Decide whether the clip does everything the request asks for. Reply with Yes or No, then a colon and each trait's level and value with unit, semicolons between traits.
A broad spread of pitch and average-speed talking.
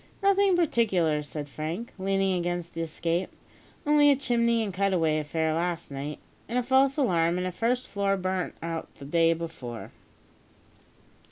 Yes: wide, 6.1 semitones; average, 165 wpm